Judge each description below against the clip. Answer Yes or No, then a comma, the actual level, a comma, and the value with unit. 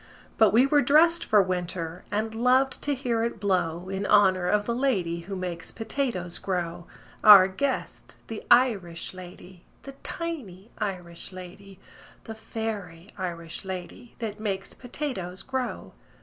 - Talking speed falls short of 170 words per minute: Yes, average, 140 wpm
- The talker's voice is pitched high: Yes, high, 200 Hz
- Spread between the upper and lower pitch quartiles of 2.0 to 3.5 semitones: No, average, 4.6 semitones